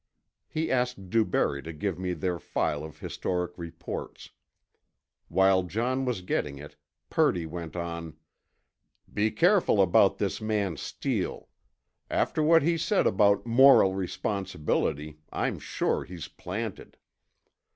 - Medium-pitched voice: No, very low, 95 Hz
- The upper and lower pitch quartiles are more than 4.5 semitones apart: Yes, wide, 5.4 semitones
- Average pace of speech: No, slow, 120 wpm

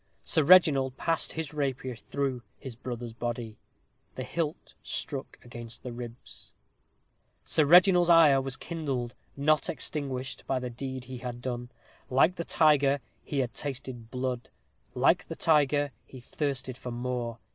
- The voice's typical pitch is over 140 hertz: No, low, 130 Hz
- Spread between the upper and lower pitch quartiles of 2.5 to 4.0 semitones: Yes, average, 3.2 semitones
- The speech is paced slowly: No, average, 145 wpm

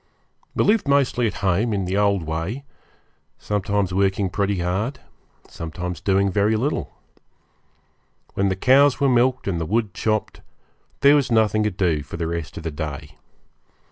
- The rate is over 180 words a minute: No, average, 160 wpm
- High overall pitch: No, low, 100 Hz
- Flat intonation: No, average, 4.7 semitones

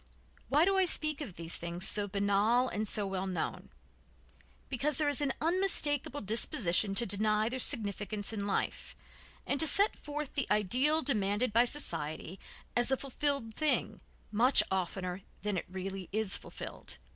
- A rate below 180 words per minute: Yes, average, 155 wpm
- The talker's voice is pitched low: No, high, 220 Hz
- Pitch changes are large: Yes, wide, 6.5 semitones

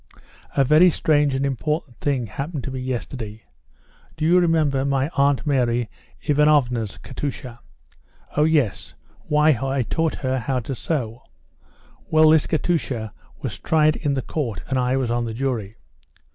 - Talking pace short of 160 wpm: Yes, average, 150 wpm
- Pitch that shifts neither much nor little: Yes, average, 3.6 semitones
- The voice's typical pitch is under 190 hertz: Yes, low, 135 Hz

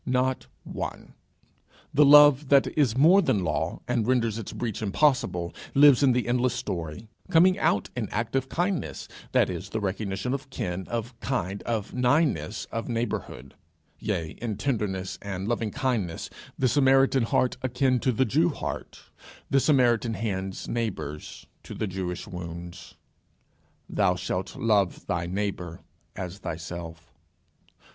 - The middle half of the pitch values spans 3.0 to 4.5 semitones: No, wide, 5.5 semitones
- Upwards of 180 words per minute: No, average, 140 wpm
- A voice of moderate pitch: No, low, 115 Hz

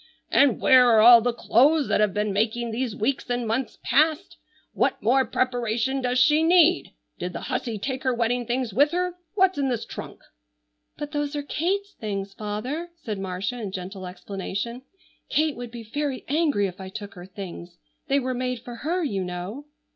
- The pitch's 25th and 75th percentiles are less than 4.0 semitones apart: No, average, 5.3 semitones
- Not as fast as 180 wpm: No, average, 185 wpm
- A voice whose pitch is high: Yes, high, 245 Hz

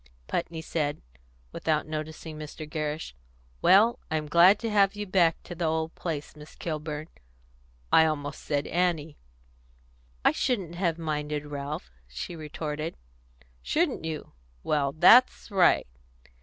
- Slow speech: Yes, slow, 125 wpm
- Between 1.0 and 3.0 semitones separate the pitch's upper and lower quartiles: Yes, narrow, 2.6 semitones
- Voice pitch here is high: No, medium, 160 Hz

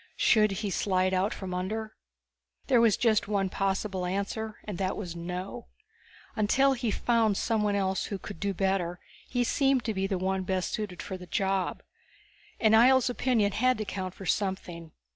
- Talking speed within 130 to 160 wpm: No, average, 175 wpm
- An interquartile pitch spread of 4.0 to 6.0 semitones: No, average, 2.8 semitones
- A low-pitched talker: No, high, 200 Hz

